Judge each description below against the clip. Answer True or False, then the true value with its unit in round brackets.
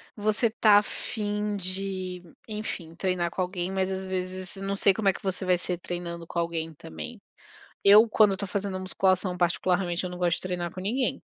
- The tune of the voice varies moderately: False (2.0 semitones)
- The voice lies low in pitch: False (185 Hz)